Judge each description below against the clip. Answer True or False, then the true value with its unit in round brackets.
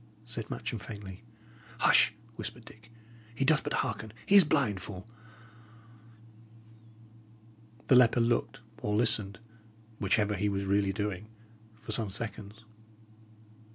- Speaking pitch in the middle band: False (110 Hz)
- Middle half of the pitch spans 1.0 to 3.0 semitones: True (2.4 semitones)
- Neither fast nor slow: False (120 wpm)